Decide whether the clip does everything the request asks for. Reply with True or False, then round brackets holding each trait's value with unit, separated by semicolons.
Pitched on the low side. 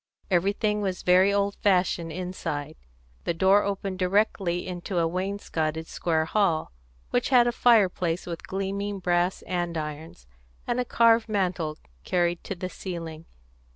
False (185 Hz)